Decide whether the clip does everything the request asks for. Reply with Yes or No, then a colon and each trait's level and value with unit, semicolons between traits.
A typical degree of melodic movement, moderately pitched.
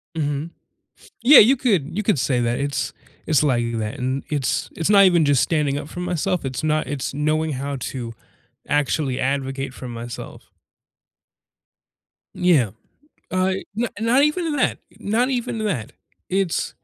No: wide, 6.2 semitones; medium, 150 Hz